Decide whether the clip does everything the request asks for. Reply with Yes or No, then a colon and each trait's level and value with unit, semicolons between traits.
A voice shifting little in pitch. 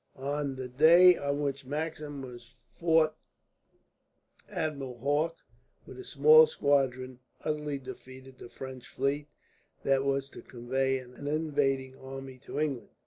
Yes: narrow, 2.2 semitones